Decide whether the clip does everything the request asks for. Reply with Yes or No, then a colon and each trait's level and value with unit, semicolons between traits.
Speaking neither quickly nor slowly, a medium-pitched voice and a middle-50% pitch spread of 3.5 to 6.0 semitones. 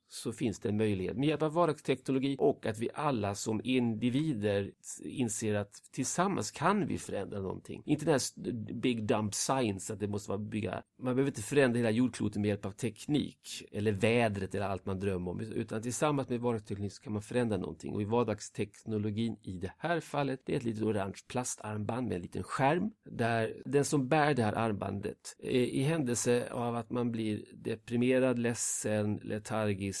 No: average, 185 wpm; low, 115 Hz; average, 3.9 semitones